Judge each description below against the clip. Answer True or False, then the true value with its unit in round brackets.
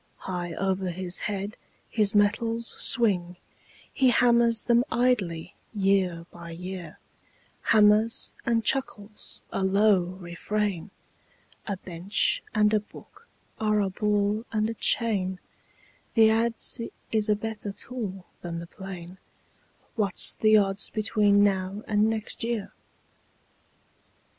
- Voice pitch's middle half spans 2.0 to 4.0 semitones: True (2.9 semitones)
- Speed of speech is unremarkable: False (120 wpm)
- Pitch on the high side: True (205 Hz)